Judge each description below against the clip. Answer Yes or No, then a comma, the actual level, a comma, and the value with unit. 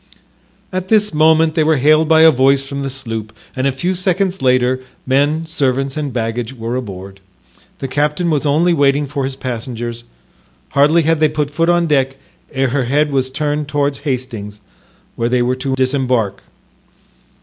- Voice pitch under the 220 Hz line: Yes, medium, 140 Hz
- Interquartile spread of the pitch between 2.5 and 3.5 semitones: Yes, average, 3.2 semitones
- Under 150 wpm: No, average, 170 wpm